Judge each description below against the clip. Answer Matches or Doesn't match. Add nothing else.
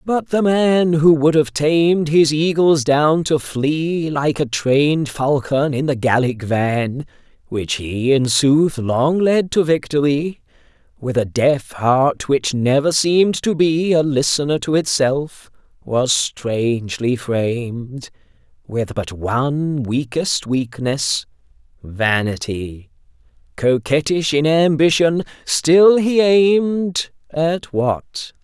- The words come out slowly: Matches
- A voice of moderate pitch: Matches